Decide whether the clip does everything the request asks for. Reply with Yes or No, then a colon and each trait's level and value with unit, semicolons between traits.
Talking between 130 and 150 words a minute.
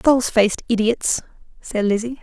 Yes: slow, 135 wpm